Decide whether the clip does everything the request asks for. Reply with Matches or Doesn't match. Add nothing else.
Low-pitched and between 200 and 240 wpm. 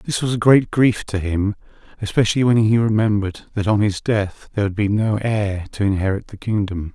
Matches